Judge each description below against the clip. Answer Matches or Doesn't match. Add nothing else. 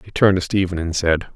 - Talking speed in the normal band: Doesn't match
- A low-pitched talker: Matches